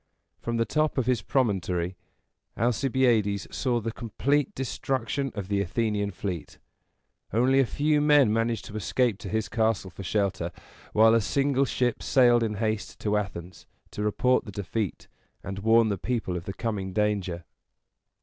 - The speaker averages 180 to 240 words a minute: No, average, 160 wpm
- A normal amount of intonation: Yes, average, 3.9 semitones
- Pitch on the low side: Yes, low, 110 Hz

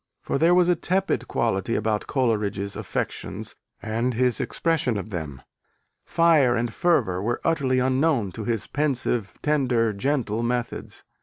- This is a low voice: Yes, low, 120 Hz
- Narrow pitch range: No, average, 5.1 semitones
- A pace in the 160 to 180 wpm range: No, average, 140 wpm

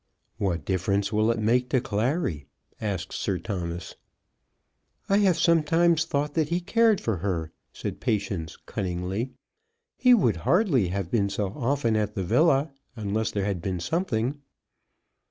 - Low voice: Yes, low, 110 Hz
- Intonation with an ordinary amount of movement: No, wide, 7.5 semitones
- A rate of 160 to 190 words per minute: No, average, 145 wpm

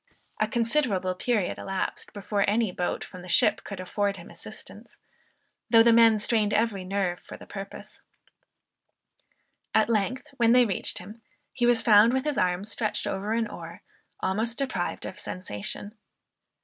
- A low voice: No, high, 210 Hz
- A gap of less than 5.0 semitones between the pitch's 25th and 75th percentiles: Yes, average, 3.6 semitones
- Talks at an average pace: Yes, average, 155 wpm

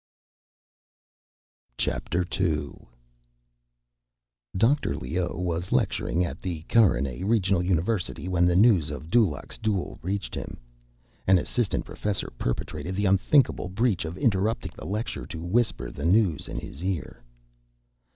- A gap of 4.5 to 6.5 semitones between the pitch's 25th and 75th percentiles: No, average, 3.8 semitones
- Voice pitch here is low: Yes, very low, 95 Hz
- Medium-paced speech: No, slow, 120 wpm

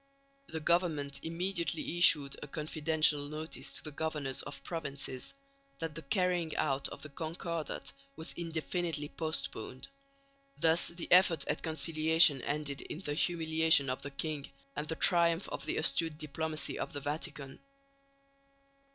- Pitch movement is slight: Yes, narrow, 2.2 semitones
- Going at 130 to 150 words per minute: Yes, average, 140 wpm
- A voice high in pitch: No, medium, 160 Hz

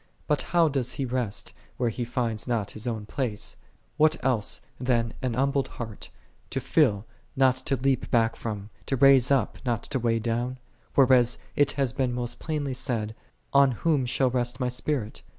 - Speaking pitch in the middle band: No, low, 125 Hz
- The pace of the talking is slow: No, average, 175 wpm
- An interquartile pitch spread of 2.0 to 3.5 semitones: Yes, average, 2.8 semitones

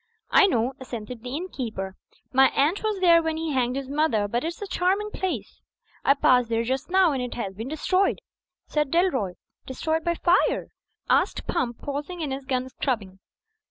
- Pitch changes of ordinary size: No, wide, 5.7 semitones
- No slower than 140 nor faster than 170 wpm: No, average, 180 wpm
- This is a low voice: No, very high, 275 Hz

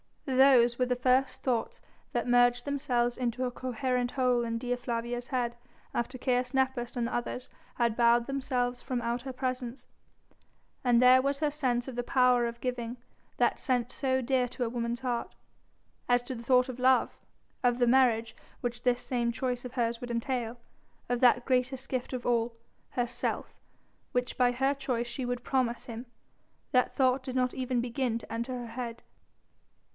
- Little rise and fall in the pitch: Yes, narrow, 1.3 semitones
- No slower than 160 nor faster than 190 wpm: Yes, average, 180 wpm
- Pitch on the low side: No, high, 245 Hz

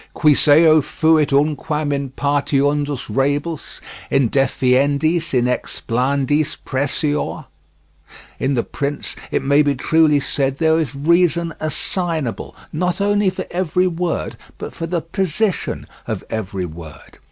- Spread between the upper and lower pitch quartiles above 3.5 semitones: No, average, 3.0 semitones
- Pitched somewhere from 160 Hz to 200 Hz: No, medium, 145 Hz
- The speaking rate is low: Yes, slow, 125 wpm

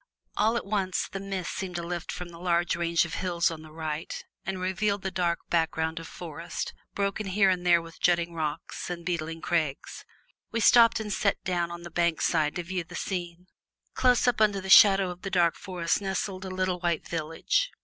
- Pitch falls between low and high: Yes, medium, 175 Hz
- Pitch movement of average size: No, narrow, 2.2 semitones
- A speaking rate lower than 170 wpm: No, fast, 205 wpm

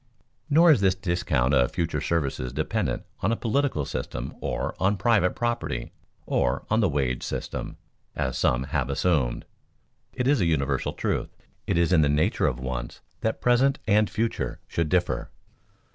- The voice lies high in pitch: No, very low, 85 Hz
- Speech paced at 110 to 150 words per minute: No, average, 160 wpm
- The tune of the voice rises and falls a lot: Yes, wide, 8.6 semitones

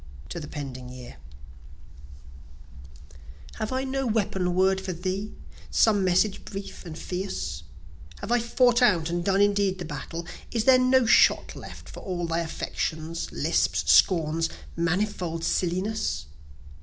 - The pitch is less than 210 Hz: Yes, medium, 185 Hz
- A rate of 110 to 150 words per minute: Yes, slow, 135 wpm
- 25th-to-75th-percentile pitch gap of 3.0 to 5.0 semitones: Yes, average, 4.3 semitones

